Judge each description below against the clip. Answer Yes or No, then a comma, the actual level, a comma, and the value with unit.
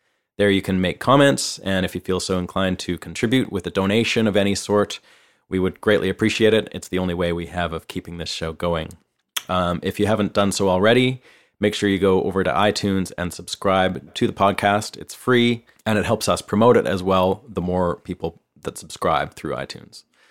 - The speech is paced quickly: Yes, fast, 210 wpm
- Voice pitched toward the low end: Yes, very low, 95 Hz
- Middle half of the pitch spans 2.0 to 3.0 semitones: Yes, narrow, 2.5 semitones